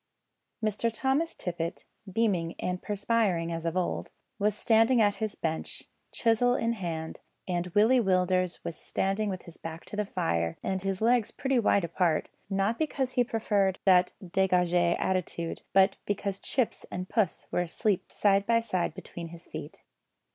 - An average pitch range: Yes, average, 4.0 semitones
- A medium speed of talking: Yes, average, 160 wpm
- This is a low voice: No, high, 195 Hz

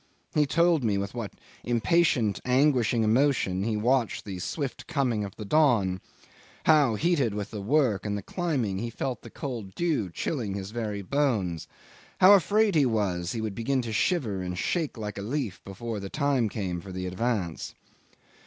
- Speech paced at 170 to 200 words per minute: Yes, average, 175 wpm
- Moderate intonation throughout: No, wide, 5.8 semitones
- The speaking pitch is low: Yes, low, 115 Hz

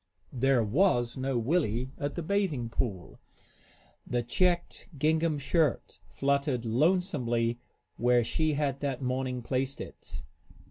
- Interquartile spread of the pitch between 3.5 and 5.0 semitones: Yes, average, 4.3 semitones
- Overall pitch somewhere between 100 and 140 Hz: Yes, low, 135 Hz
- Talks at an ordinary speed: No, slow, 120 wpm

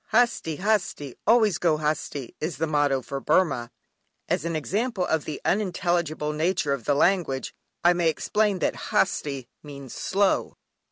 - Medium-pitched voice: Yes, medium, 160 Hz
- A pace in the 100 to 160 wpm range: Yes, average, 150 wpm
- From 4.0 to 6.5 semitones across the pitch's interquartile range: Yes, average, 4.6 semitones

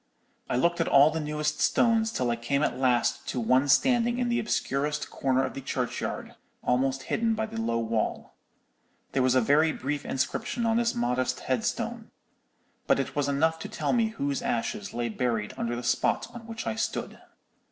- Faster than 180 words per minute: Yes, average, 190 wpm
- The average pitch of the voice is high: No, medium, 140 Hz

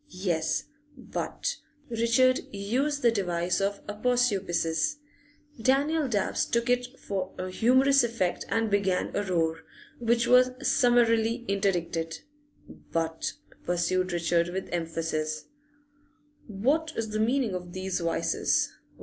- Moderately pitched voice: No, high, 200 Hz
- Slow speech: Yes, slow, 115 wpm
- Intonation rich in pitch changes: Yes, wide, 5.7 semitones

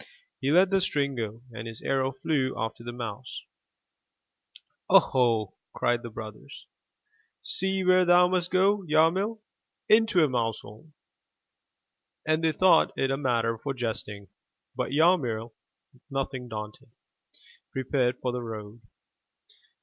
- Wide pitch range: Yes, wide, 6.7 semitones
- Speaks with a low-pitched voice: Yes, low, 130 Hz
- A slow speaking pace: Yes, slow, 125 wpm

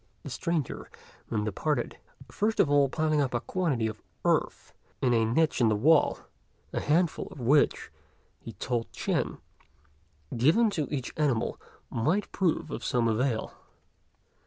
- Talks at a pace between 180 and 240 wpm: No, average, 145 wpm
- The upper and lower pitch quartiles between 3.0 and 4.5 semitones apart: No, average, 5.3 semitones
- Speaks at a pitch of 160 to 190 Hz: No, medium, 140 Hz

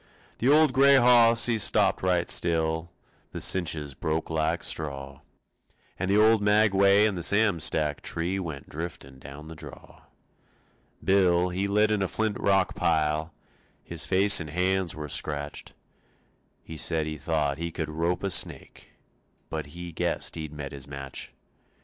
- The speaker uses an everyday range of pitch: Yes, average, 4.2 semitones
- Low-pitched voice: Yes, very low, 85 Hz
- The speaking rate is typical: Yes, average, 155 wpm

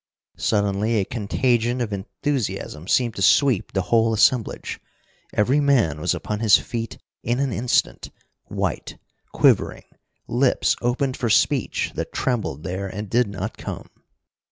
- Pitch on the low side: Yes, low, 115 Hz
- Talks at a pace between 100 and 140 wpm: Yes, slow, 135 wpm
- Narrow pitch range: No, average, 3.6 semitones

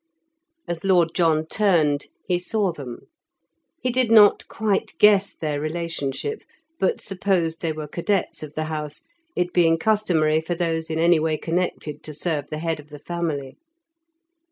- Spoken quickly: No, average, 155 wpm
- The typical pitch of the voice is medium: Yes, medium, 165 Hz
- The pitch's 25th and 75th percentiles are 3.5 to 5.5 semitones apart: No, average, 3.0 semitones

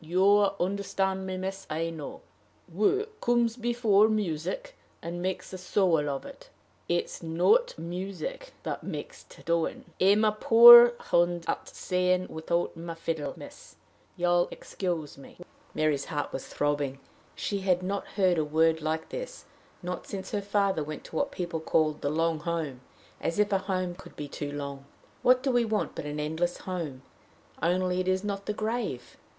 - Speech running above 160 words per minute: Yes, average, 170 wpm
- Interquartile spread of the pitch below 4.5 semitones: Yes, average, 4.0 semitones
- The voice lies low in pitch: No, medium, 180 Hz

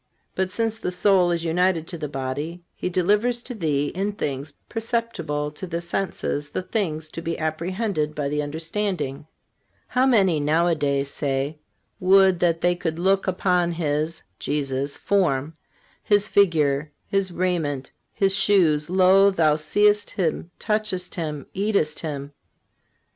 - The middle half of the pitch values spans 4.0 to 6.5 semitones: Yes, average, 4.4 semitones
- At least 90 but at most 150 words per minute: Yes, average, 140 wpm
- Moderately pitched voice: Yes, medium, 170 Hz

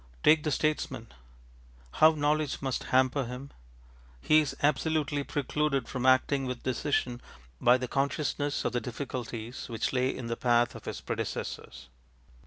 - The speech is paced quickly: No, average, 145 wpm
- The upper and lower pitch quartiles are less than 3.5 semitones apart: Yes, average, 2.9 semitones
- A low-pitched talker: Yes, low, 130 Hz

